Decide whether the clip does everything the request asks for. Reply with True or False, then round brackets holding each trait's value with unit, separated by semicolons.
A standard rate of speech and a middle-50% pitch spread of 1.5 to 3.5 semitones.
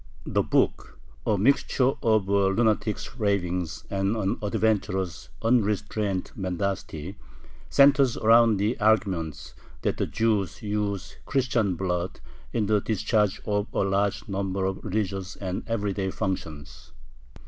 False (120 wpm; 2.4 semitones)